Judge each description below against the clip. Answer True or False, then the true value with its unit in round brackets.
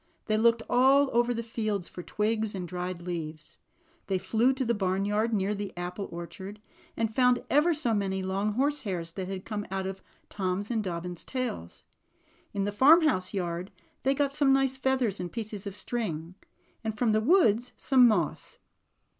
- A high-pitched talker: True (210 Hz)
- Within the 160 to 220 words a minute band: True (170 wpm)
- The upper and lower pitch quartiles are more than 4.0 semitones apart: True (4.6 semitones)